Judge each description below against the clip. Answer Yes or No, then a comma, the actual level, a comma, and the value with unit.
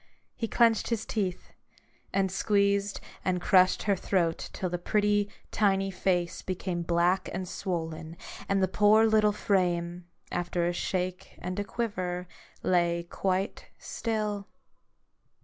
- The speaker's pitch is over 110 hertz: Yes, high, 190 Hz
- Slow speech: Yes, slow, 130 wpm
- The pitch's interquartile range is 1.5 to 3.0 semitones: Yes, narrow, 2.6 semitones